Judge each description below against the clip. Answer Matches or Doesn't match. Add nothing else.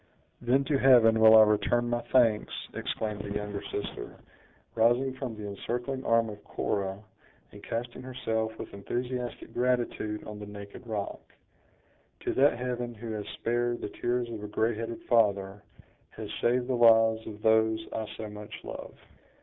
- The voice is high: Doesn't match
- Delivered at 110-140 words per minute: Doesn't match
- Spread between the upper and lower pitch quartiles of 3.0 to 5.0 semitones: Doesn't match